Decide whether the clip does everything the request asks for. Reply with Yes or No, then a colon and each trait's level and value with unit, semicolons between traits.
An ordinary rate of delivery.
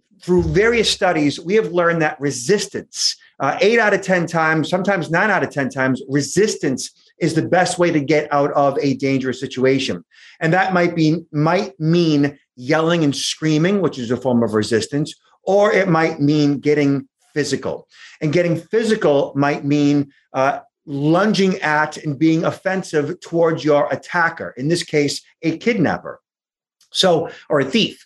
Yes: average, 165 wpm